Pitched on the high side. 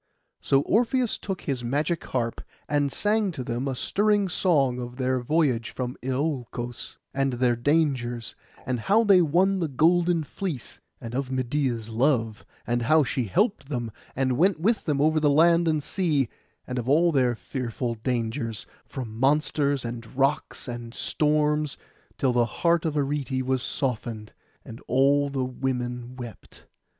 No: low, 135 Hz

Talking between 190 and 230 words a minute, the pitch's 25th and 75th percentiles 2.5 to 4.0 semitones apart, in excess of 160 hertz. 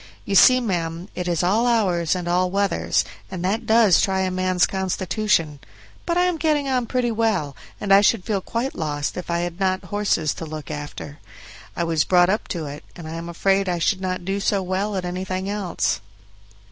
Yes: fast, 205 wpm; average, 3.3 semitones; medium, 185 Hz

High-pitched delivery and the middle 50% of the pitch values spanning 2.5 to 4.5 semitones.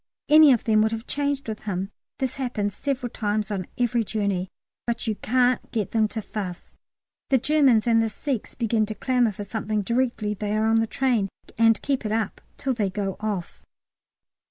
Yes: high, 220 Hz; average, 3.0 semitones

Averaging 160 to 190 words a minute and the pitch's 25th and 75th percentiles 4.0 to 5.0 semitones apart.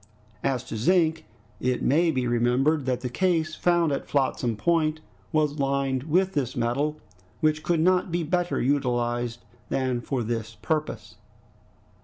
No: average, 145 wpm; average, 4.6 semitones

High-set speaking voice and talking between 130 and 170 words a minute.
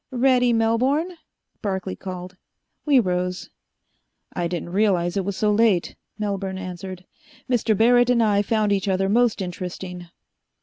Yes: high, 200 Hz; average, 140 wpm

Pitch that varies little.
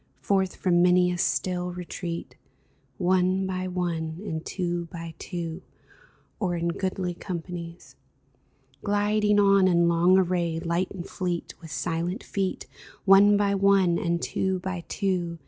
Yes: narrow, 1.9 semitones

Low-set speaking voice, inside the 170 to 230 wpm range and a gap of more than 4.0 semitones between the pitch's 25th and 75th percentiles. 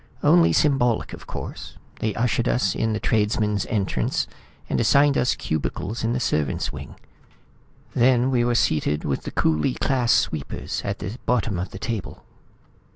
No: low, 110 Hz; average, 160 wpm; average, 4.7 semitones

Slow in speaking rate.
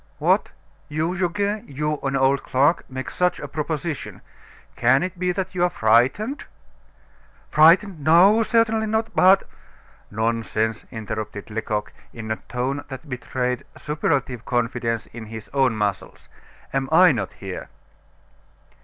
Yes: slow, 130 wpm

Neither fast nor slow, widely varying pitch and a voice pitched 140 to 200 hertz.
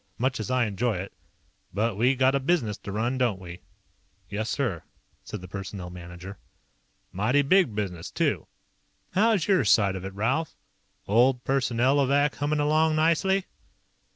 No: average, 150 wpm; wide, 6.2 semitones; low, 120 Hz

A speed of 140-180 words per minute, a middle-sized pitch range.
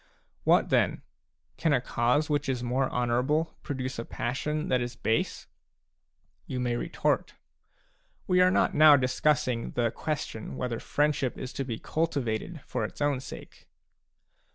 Yes: average, 150 wpm; average, 3.6 semitones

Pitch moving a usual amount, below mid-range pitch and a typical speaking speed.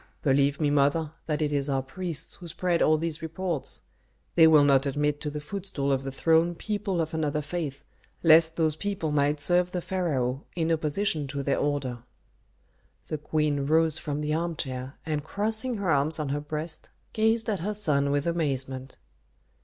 No: average, 3.0 semitones; medium, 155 Hz; average, 175 wpm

